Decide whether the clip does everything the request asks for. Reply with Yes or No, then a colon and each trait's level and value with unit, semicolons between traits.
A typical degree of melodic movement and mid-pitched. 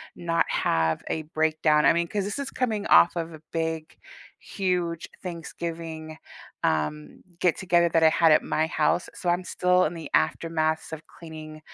No: narrow, 1.7 semitones; medium, 165 Hz